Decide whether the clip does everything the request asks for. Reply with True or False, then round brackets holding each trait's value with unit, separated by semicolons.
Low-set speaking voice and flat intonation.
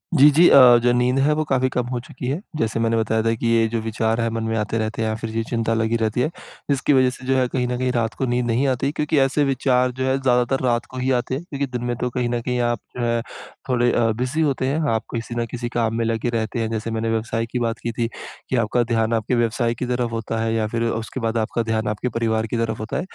True (120 Hz; 2.0 semitones)